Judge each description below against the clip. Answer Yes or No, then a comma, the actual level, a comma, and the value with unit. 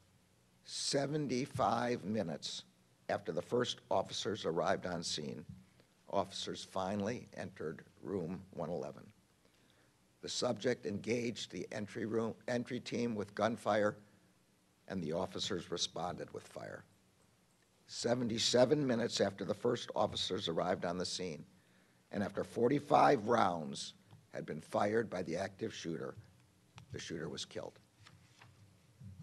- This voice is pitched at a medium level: No, low, 105 Hz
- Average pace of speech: No, slow, 115 wpm